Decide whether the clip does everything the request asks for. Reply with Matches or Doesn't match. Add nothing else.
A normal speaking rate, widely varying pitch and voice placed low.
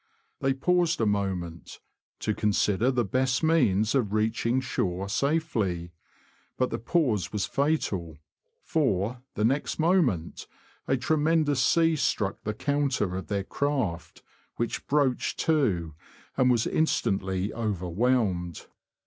Doesn't match